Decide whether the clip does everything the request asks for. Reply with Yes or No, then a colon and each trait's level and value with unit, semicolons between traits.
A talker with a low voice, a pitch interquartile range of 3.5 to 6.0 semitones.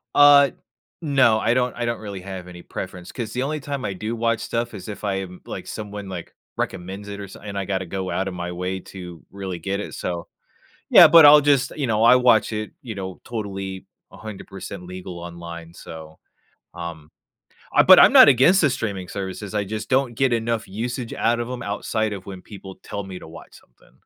Yes: low, 100 Hz; average, 4.1 semitones